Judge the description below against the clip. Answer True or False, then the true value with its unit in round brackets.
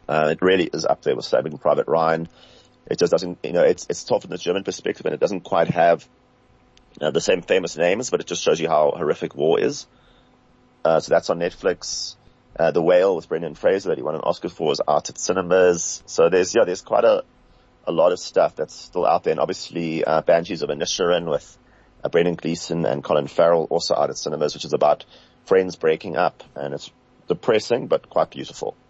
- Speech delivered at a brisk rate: True (220 wpm)